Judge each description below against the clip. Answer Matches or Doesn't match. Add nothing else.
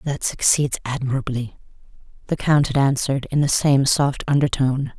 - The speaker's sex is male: Doesn't match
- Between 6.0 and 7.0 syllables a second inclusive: Doesn't match